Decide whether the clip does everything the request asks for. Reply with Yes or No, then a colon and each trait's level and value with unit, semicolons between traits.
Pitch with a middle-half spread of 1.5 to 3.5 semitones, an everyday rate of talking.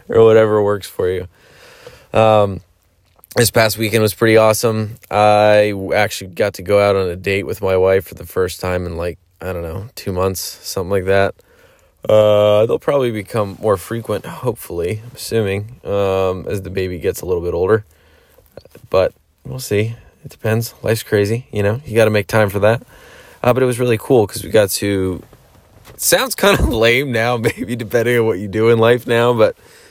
Yes: average, 2.9 semitones; average, 195 wpm